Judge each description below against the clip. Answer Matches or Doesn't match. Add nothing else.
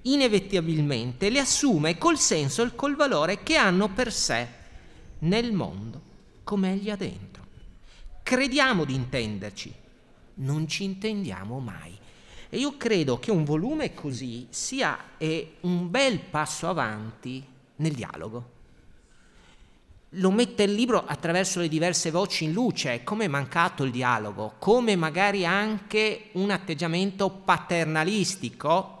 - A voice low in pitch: Doesn't match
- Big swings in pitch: Matches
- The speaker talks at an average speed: Matches